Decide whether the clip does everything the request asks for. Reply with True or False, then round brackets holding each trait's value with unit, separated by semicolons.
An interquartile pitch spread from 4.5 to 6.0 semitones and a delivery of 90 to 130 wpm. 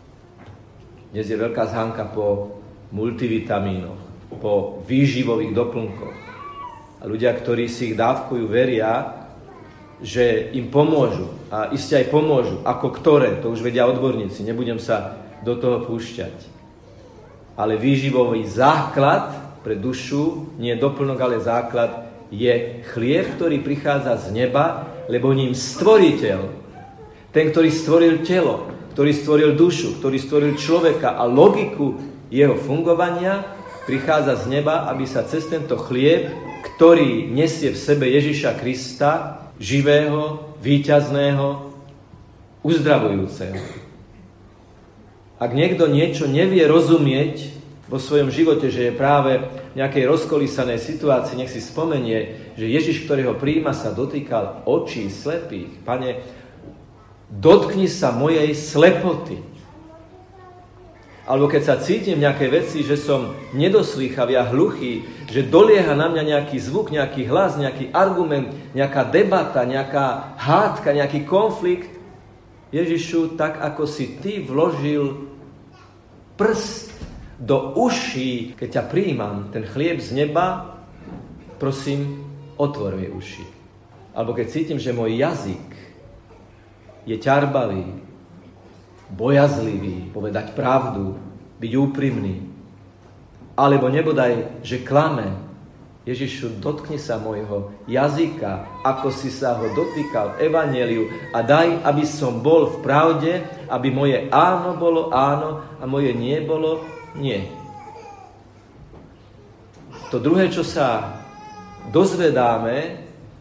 True (5.0 semitones; 115 wpm)